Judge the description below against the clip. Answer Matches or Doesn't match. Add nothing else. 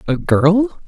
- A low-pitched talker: Doesn't match